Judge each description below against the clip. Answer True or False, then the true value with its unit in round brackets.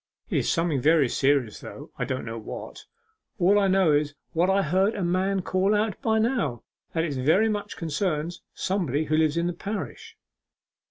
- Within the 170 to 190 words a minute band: True (180 wpm)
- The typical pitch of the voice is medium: True (170 Hz)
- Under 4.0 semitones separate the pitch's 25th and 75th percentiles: False (4.8 semitones)